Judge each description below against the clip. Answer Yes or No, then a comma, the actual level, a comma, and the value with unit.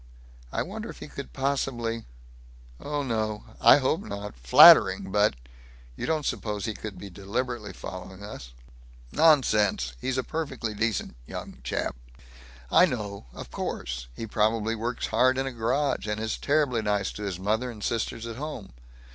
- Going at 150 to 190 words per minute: Yes, average, 160 wpm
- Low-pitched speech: Yes, low, 110 Hz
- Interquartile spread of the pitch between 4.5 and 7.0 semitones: No, average, 4.0 semitones